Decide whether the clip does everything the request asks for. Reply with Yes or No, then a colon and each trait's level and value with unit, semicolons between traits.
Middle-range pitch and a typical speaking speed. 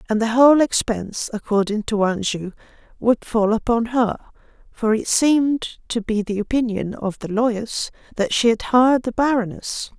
No: high, 225 Hz; average, 170 wpm